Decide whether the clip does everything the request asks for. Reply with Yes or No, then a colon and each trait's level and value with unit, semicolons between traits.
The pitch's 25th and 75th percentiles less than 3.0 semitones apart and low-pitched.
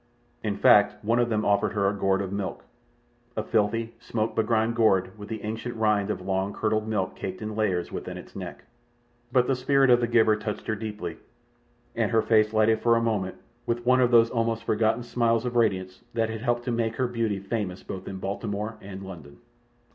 Yes: narrow, 2.5 semitones; low, 110 Hz